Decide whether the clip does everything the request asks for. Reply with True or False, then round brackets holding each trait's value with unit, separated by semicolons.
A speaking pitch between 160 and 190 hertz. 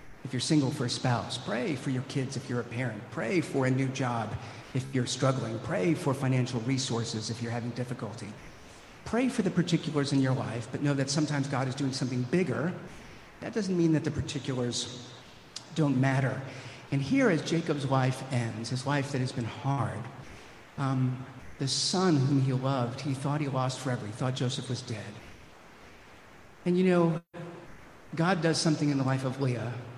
False (135 Hz)